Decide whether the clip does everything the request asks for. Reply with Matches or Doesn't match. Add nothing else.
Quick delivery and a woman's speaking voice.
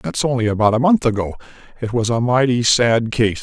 Doesn't match